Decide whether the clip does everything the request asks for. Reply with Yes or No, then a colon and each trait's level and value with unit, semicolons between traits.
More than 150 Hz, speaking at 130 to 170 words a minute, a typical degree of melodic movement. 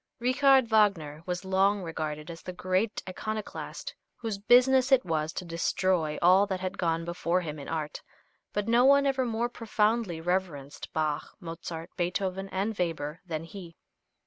Yes: medium, 185 Hz; average, 155 wpm; average, 4.7 semitones